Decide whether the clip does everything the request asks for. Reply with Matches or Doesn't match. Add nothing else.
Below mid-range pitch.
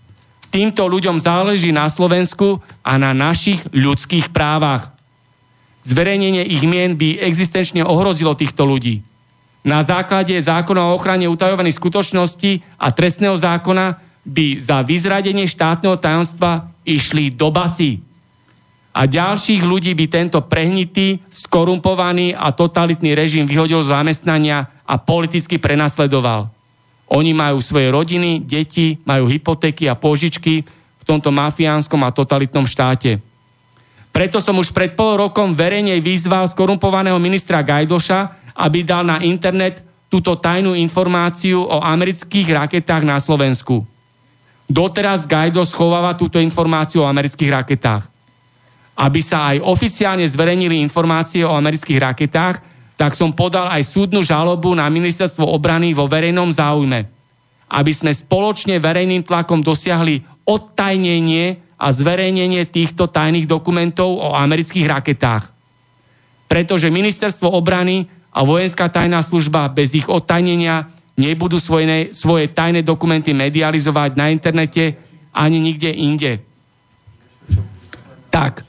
Doesn't match